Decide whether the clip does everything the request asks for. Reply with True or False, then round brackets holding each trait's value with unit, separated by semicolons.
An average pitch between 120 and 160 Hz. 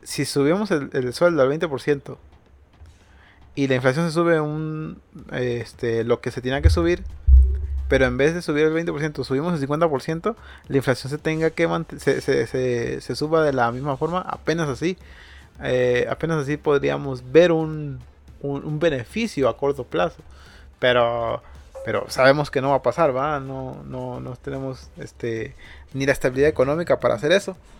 True (135 Hz)